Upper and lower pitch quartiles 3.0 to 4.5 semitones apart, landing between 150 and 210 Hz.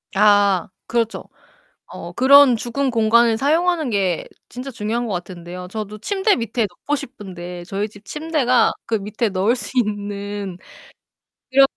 No: average, 4.2 semitones; high, 220 Hz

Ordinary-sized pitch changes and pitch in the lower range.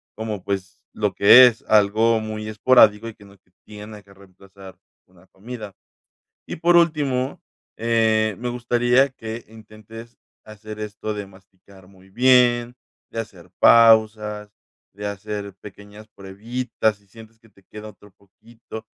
No: narrow, 2.3 semitones; low, 110 Hz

